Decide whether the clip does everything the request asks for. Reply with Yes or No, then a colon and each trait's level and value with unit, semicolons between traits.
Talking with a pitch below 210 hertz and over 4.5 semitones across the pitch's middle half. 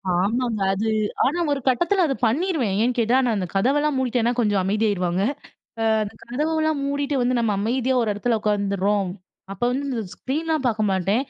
No: high, 235 Hz; average, 4.9 semitones